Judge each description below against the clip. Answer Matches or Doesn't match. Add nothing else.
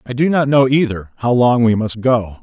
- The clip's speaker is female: Doesn't match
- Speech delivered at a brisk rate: Matches